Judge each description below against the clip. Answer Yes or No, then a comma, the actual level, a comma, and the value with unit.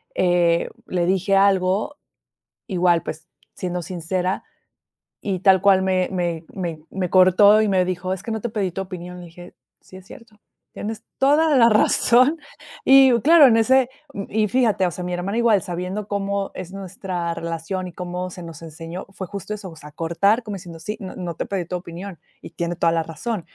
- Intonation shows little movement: No, average, 3.0 semitones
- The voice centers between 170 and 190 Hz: Yes, medium, 185 Hz